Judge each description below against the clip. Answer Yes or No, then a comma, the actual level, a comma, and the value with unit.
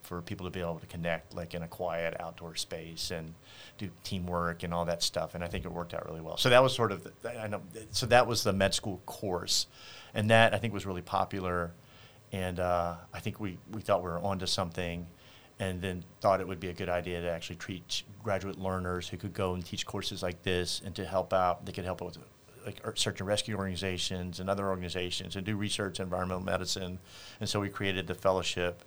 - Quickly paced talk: Yes, fast, 235 wpm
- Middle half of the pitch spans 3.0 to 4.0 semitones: No, narrow, 2.4 semitones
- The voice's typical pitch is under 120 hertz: Yes, very low, 95 Hz